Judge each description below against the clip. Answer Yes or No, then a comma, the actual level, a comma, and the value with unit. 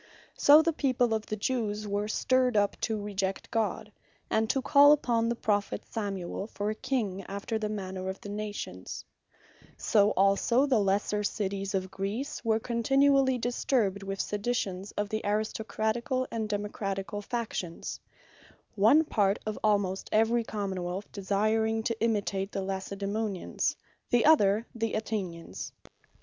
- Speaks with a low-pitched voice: No, high, 210 Hz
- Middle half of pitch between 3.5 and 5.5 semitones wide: No, average, 2.7 semitones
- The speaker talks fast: No, average, 140 wpm